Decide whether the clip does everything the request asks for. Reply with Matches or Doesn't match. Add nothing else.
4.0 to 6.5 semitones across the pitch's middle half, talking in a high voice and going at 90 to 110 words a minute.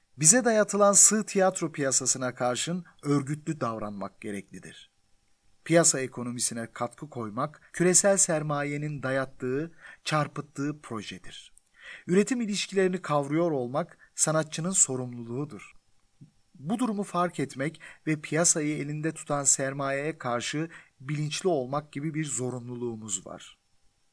Doesn't match